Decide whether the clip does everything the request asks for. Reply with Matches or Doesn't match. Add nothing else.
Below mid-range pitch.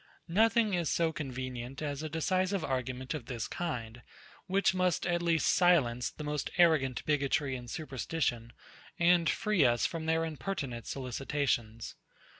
Doesn't match